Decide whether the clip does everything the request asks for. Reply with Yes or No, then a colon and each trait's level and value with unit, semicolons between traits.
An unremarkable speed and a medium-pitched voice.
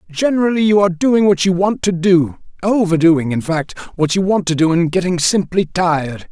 Yes: average, 190 wpm; medium, 175 Hz